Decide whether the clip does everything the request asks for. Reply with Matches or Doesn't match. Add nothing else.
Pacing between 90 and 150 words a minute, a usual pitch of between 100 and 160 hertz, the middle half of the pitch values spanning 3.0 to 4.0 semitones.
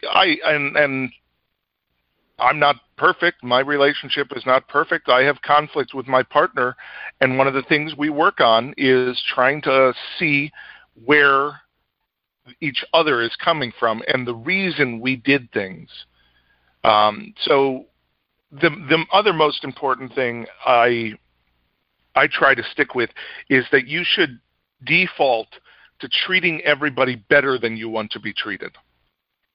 Matches